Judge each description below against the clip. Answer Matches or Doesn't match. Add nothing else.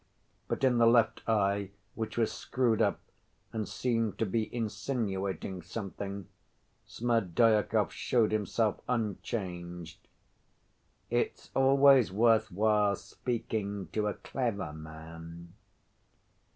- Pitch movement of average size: Matches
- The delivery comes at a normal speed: Doesn't match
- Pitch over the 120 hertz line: Doesn't match